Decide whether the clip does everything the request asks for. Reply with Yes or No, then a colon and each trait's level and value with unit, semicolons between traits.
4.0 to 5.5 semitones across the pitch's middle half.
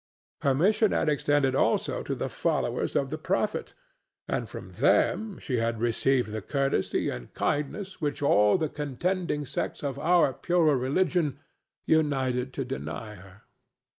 Yes: average, 4.3 semitones